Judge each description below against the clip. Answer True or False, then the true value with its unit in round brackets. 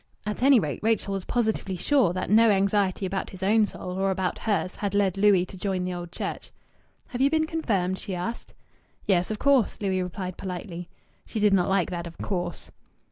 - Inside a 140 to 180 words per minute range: False (200 wpm)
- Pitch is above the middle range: True (195 Hz)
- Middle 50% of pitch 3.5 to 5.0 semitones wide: False (2.8 semitones)